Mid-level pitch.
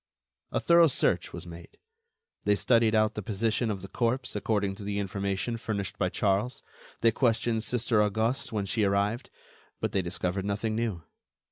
No: low, 105 Hz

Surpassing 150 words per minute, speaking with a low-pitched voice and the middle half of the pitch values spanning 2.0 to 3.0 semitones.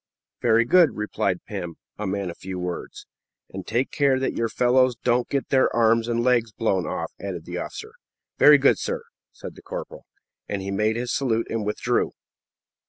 No: average, 180 wpm; low, 115 Hz; average, 4.4 semitones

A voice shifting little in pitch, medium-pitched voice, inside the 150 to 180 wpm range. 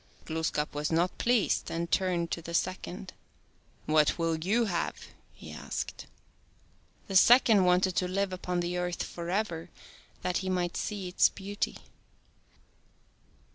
No: narrow, 2.2 semitones; medium, 180 Hz; average, 140 wpm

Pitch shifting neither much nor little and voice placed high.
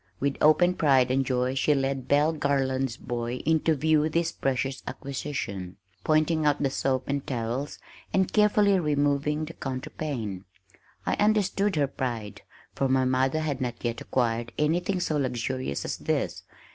No: average, 3.3 semitones; medium, 140 Hz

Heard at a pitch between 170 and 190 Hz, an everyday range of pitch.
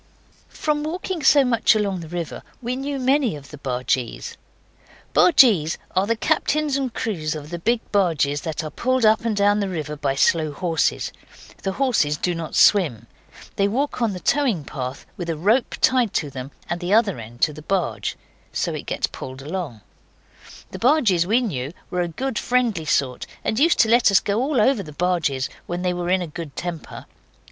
No: medium, 185 Hz; wide, 7.6 semitones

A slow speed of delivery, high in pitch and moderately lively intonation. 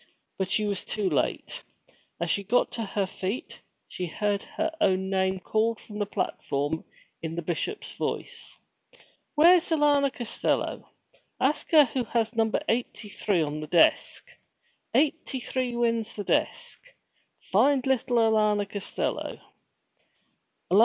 Yes: slow, 130 wpm; high, 220 Hz; average, 4.9 semitones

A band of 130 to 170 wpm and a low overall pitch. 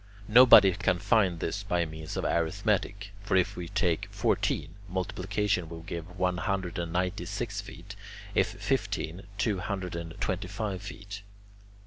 Yes: average, 150 wpm; very low, 95 Hz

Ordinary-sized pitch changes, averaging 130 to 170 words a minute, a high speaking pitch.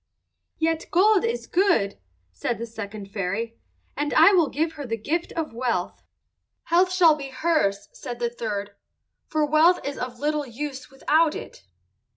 No: wide, 6.2 semitones; average, 160 wpm; very high, 285 Hz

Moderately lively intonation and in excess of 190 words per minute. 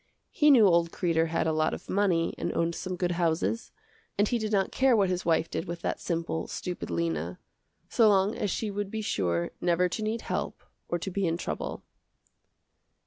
Yes: average, 3.8 semitones; average, 200 wpm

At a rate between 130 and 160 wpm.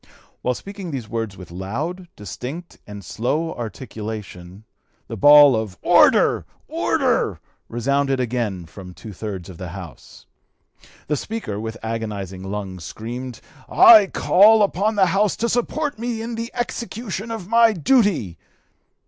Yes: average, 140 wpm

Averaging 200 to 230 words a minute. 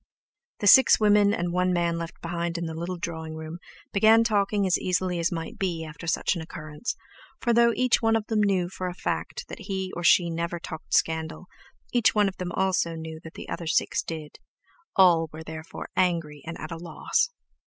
Yes: fast, 205 wpm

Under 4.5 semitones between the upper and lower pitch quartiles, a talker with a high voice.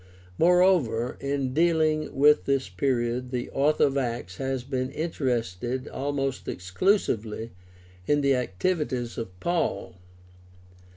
No: average, 3.8 semitones; low, 135 Hz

